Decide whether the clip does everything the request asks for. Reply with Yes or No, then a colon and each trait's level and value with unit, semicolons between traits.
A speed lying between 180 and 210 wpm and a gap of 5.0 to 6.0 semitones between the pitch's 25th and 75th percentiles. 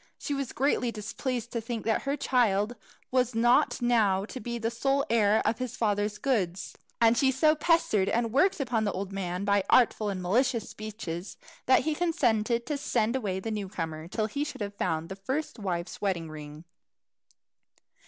No: average, 185 wpm; average, 4.3 semitones